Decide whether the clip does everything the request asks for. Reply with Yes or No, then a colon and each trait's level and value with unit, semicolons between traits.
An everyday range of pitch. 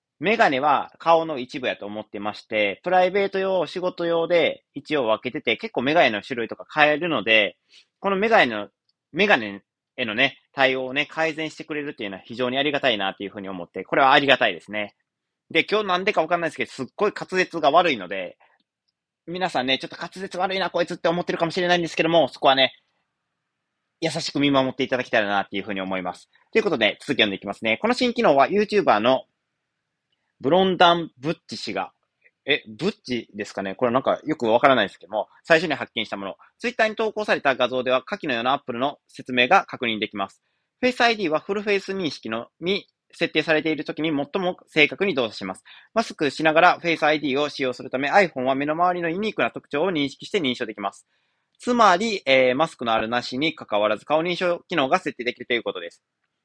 No: wide, 6.3 semitones